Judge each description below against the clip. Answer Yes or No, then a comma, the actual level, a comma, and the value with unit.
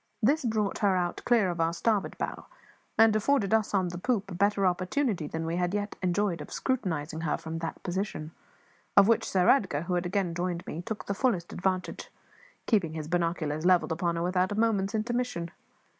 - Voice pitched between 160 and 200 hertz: Yes, medium, 185 Hz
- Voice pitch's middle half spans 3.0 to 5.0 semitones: Yes, average, 3.7 semitones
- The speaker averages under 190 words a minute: No, average, 195 wpm